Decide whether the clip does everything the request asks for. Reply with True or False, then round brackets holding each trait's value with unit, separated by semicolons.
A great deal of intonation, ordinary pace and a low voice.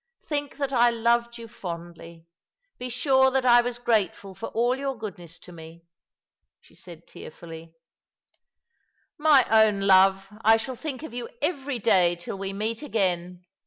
False (5.8 semitones; 160 wpm; 225 Hz)